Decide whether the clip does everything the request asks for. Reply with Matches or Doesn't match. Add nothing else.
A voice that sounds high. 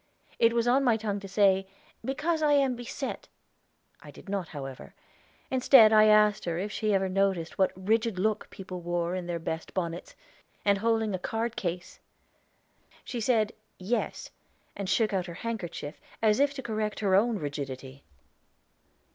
Matches